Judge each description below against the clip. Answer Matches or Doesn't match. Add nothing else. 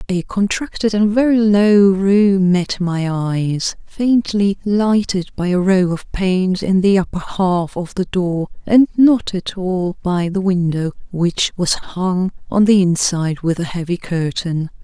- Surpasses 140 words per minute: Matches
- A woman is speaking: Matches